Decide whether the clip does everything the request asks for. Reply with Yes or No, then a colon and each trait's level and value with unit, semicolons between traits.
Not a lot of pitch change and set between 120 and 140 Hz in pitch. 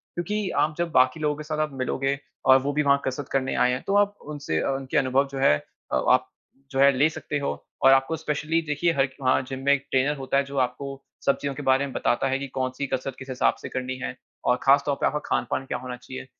Yes: narrow, 2.1 semitones; low, 135 Hz